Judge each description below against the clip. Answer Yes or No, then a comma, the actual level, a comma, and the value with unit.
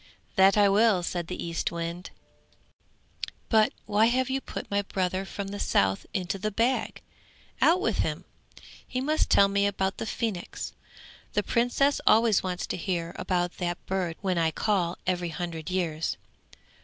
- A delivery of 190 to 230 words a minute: No, average, 155 wpm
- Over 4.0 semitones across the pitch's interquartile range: No, average, 3.5 semitones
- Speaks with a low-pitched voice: No, high, 190 Hz